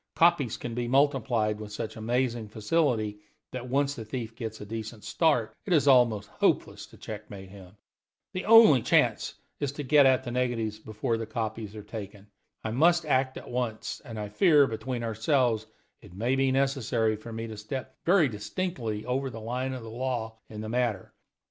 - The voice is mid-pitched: No, low, 115 Hz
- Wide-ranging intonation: No, average, 3.4 semitones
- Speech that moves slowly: No, average, 180 wpm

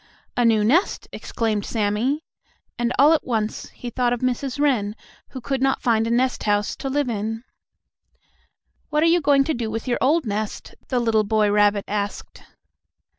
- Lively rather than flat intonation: No, average, 4.0 semitones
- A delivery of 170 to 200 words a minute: Yes, average, 175 wpm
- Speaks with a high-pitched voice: Yes, high, 235 Hz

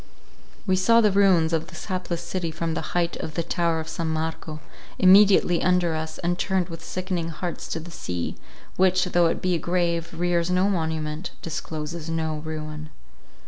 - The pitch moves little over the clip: Yes, narrow, 2.2 semitones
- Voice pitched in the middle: Yes, medium, 170 Hz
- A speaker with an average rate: Yes, average, 180 wpm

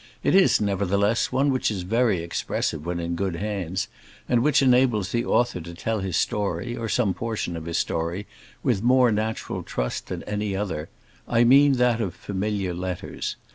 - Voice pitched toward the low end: Yes, low, 105 Hz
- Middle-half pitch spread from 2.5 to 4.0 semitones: No, average, 4.6 semitones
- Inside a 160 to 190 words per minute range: Yes, average, 175 wpm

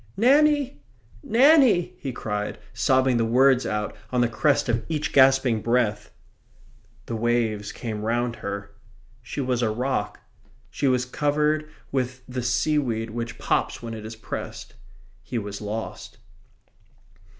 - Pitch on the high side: No, low, 125 Hz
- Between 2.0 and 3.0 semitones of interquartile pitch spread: No, average, 3.9 semitones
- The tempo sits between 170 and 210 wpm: No, slow, 135 wpm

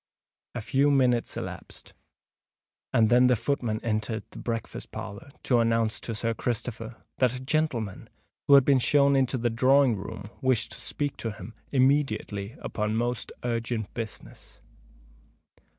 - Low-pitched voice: Yes, low, 120 Hz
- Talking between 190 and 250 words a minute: No, average, 145 wpm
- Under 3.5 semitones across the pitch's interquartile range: Yes, average, 2.9 semitones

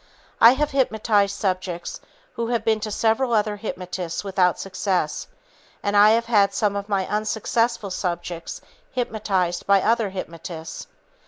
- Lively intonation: No, average, 3.3 semitones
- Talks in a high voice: Yes, high, 205 Hz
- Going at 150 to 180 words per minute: No, average, 140 wpm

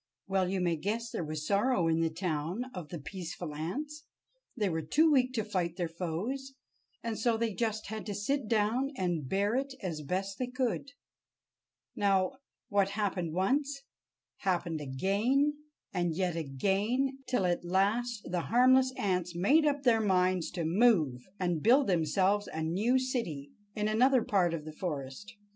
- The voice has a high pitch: Yes, high, 195 Hz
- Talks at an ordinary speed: Yes, average, 165 wpm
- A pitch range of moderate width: No, wide, 5.9 semitones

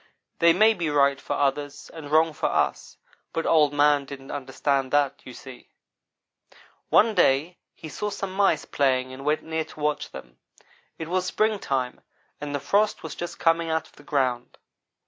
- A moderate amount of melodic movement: Yes, average, 3.2 semitones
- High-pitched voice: No, medium, 150 Hz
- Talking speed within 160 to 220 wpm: Yes, average, 175 wpm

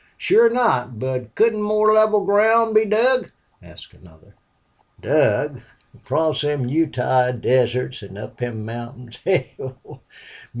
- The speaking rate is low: Yes, slow, 120 wpm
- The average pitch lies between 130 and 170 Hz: Yes, medium, 140 Hz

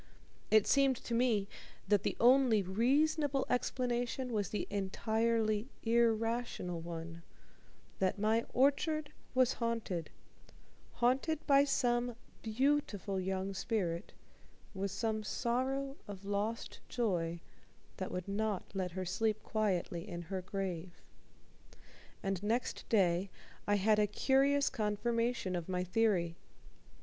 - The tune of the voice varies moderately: Yes, average, 4.3 semitones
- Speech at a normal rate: No, slow, 115 wpm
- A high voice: Yes, high, 215 Hz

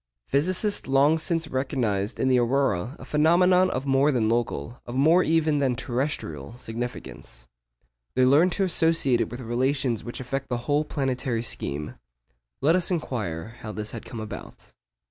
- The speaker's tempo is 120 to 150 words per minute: No, average, 160 wpm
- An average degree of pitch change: Yes, average, 4.3 semitones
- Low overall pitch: Yes, low, 130 Hz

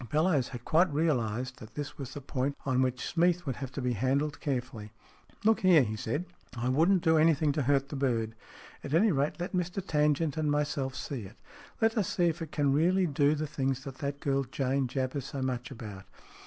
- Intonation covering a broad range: No, average, 3.5 semitones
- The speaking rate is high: Yes, fast, 215 wpm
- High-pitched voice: No, medium, 140 Hz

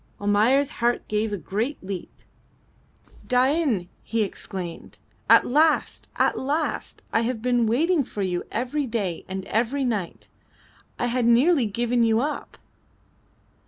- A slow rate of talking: Yes, slow, 130 wpm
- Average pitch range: Yes, average, 4.4 semitones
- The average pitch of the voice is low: No, high, 235 Hz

